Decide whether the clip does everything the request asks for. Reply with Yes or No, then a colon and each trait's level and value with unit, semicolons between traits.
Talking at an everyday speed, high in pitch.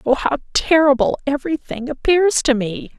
Yes: average, 160 wpm; very high, 285 Hz